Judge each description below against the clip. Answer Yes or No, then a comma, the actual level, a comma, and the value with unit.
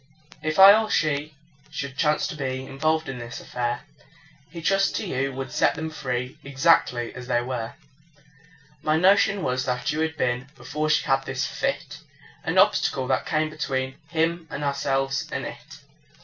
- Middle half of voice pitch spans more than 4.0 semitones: No, average, 3.5 semitones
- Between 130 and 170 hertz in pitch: Yes, medium, 140 Hz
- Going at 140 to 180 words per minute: Yes, average, 170 wpm